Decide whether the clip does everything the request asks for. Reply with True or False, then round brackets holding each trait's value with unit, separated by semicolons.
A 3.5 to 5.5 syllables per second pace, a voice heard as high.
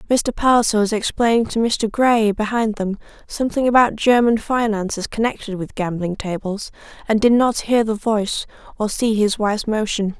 True (5.2 syllables/s; 220 Hz)